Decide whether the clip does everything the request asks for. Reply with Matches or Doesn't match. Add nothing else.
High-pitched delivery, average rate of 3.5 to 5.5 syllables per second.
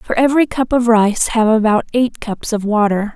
Matches